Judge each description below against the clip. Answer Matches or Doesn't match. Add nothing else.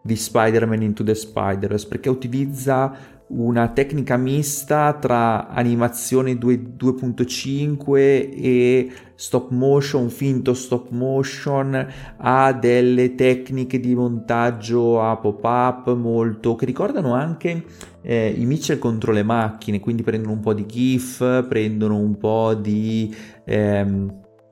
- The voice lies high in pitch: Doesn't match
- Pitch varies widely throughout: Doesn't match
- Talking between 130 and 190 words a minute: Doesn't match